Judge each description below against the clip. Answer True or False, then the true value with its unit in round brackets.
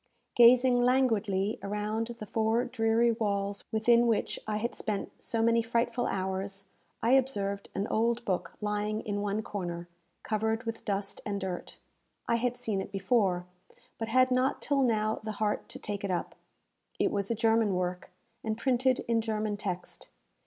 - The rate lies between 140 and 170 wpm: True (165 wpm)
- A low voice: False (220 Hz)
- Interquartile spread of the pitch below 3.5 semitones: True (2.6 semitones)